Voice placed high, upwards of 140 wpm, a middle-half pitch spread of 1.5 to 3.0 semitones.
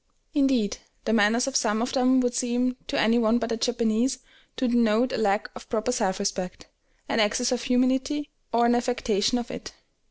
Yes: high, 240 Hz; average, 190 wpm; narrow, 2.5 semitones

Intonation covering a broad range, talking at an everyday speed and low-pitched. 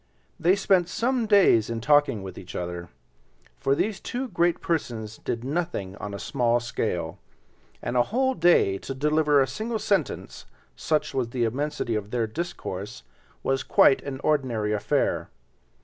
Yes: wide, 7.9 semitones; average, 150 wpm; low, 130 Hz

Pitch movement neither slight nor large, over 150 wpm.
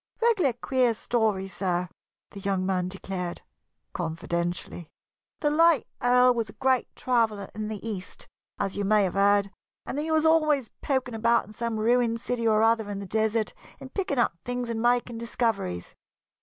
Yes: average, 3.9 semitones; average, 170 wpm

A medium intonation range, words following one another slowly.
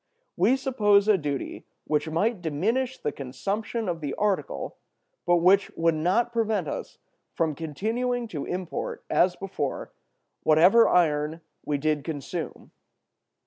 No: wide, 6.0 semitones; slow, 130 wpm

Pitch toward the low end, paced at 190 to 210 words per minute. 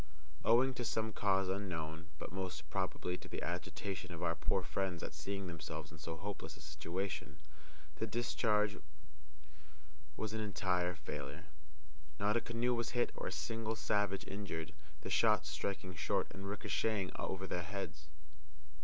No: very low, 95 Hz; average, 155 wpm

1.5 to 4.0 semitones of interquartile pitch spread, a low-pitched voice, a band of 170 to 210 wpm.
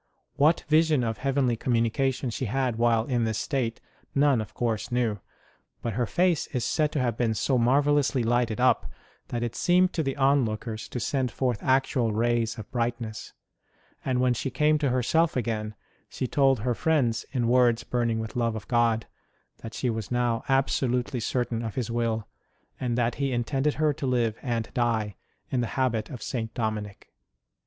Yes: average, 2.8 semitones; low, 120 Hz; average, 180 wpm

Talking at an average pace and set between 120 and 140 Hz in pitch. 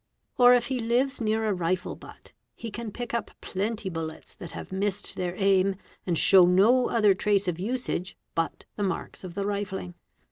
No: average, 185 wpm; high, 200 Hz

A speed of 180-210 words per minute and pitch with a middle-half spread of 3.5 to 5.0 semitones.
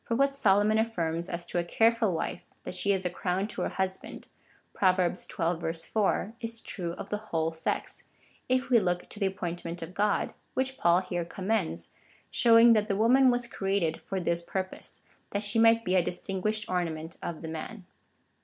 Yes: average, 190 wpm; average, 4.2 semitones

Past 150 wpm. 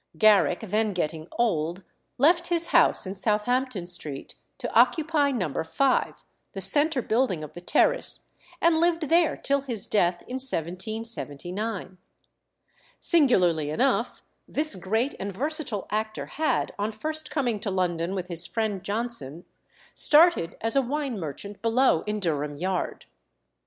No: slow, 135 wpm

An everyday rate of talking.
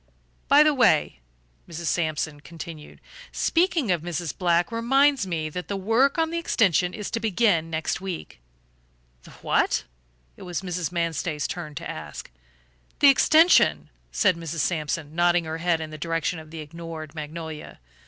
Yes: average, 155 wpm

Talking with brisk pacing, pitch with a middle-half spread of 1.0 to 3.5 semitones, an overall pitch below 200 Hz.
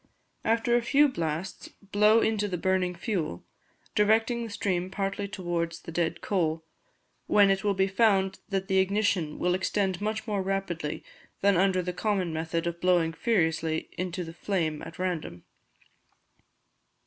No: average, 150 wpm; average, 3.2 semitones; high, 190 Hz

